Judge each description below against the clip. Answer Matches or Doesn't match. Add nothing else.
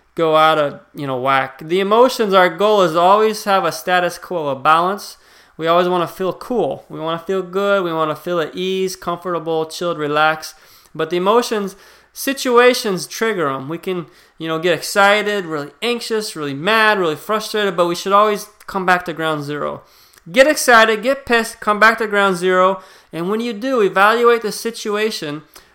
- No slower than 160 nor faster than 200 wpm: Matches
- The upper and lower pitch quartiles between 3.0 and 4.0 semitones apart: Doesn't match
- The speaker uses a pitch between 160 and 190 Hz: Matches